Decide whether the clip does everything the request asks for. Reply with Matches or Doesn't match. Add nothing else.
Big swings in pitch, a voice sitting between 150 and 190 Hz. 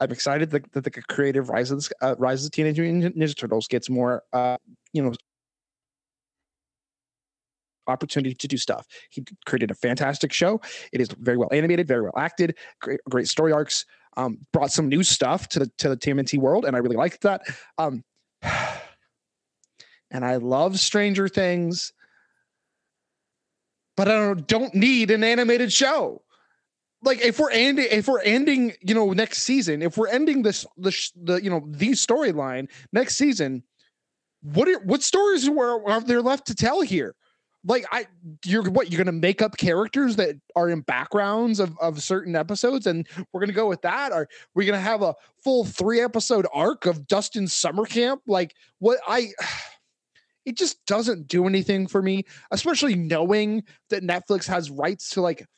Matches